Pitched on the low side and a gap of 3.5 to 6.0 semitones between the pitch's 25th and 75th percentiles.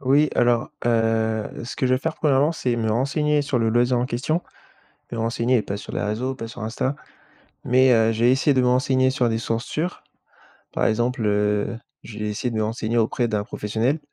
No: low, 120 Hz; average, 2.7 semitones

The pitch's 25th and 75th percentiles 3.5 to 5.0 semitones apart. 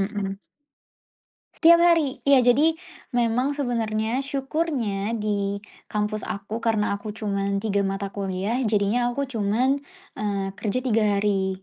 Yes: average, 3.9 semitones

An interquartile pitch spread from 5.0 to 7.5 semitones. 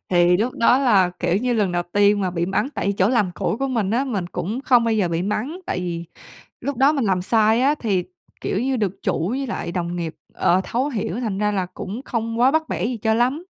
Yes: average, 5.3 semitones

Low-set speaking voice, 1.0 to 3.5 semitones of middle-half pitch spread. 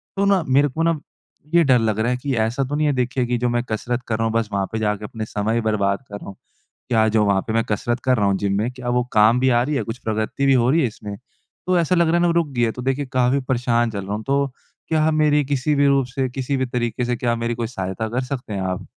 No: low, 120 Hz; average, 3.9 semitones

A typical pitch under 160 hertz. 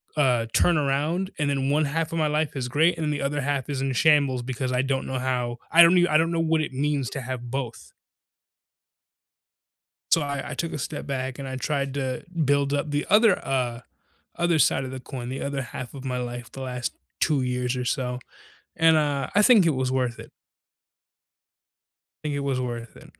Yes: medium, 140 Hz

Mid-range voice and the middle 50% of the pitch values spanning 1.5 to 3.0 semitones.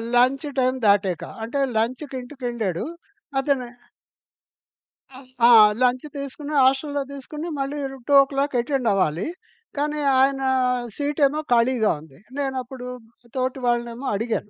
No: very high, 260 Hz; average, 2.7 semitones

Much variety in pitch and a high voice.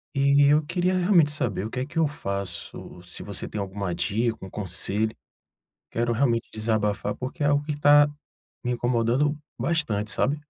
No: wide, 6.0 semitones; low, 120 Hz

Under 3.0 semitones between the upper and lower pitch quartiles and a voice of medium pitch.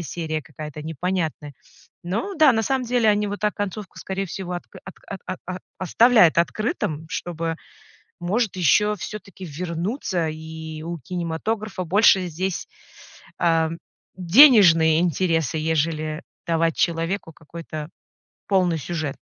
No: average, 3.9 semitones; medium, 175 Hz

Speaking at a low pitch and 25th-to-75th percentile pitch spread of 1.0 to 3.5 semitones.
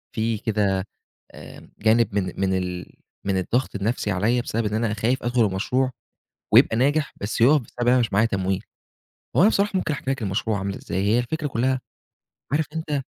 No: low, 115 Hz; average, 4.4 semitones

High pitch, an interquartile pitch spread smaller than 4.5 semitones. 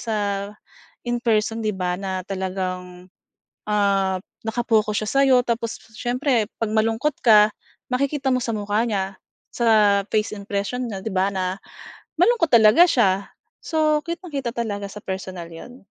Yes: high, 215 Hz; average, 3.9 semitones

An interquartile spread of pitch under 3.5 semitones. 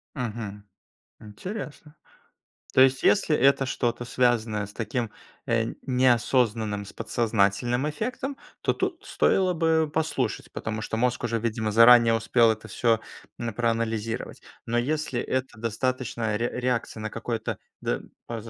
Yes: average, 2.8 semitones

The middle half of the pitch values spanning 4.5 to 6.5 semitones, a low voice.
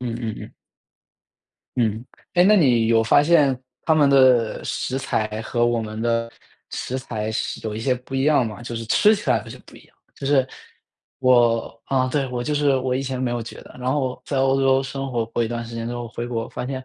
No: narrow, 2.6 semitones; low, 125 Hz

